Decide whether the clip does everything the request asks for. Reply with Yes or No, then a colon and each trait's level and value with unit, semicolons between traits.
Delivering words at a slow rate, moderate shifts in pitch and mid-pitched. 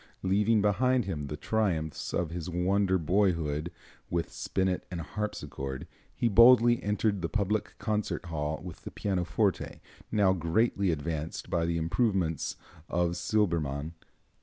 No: slow, 130 wpm; average, 4.2 semitones; very low, 90 Hz